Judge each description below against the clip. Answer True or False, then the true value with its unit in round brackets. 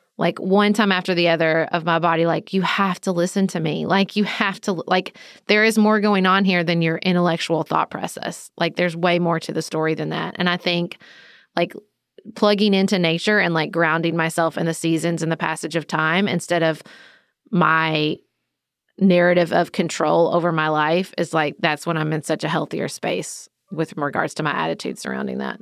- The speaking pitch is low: False (170 Hz)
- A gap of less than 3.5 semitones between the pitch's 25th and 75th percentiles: True (2.7 semitones)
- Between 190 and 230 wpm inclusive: True (200 wpm)